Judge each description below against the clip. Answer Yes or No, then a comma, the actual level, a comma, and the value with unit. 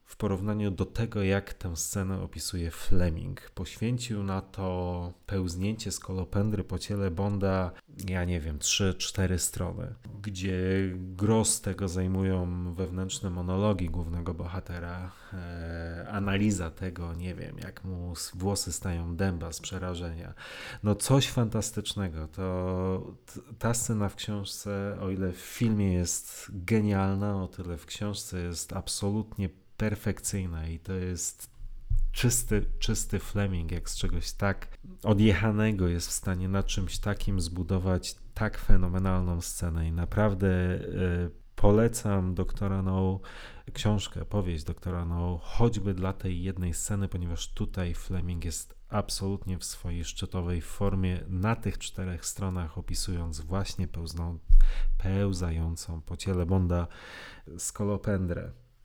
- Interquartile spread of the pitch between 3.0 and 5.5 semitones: No, narrow, 2.5 semitones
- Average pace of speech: Yes, average, 120 wpm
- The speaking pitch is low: Yes, very low, 95 Hz